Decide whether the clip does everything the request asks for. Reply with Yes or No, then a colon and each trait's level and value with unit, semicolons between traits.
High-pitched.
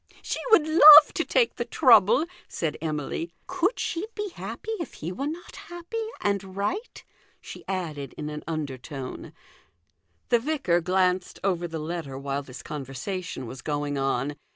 No: medium, 175 Hz